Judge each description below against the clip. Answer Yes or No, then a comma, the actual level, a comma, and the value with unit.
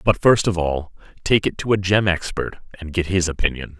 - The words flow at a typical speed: No, fast, 220 wpm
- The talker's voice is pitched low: Yes, very low, 90 Hz